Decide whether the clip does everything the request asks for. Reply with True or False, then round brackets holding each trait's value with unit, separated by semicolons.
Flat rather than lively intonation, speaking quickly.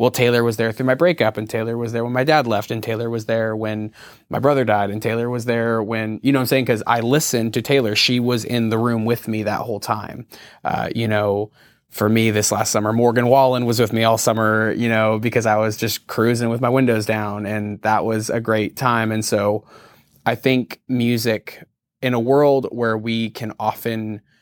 True (1.8 semitones; 225 wpm)